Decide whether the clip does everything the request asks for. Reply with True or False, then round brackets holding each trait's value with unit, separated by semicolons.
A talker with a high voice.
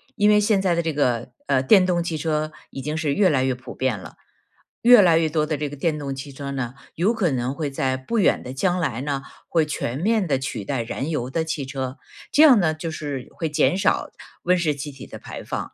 False (150 Hz)